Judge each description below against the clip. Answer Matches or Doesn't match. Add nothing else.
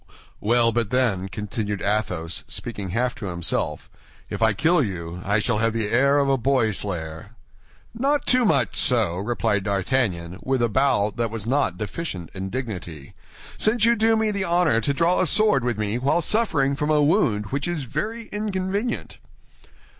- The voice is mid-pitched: Doesn't match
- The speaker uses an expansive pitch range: Matches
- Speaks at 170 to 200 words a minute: Matches